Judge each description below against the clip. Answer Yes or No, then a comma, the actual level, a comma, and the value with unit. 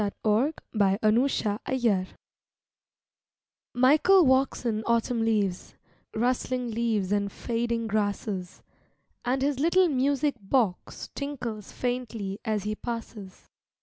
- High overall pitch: Yes, high, 230 Hz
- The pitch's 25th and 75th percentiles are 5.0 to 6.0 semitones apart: No, average, 3.7 semitones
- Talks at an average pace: No, slow, 110 wpm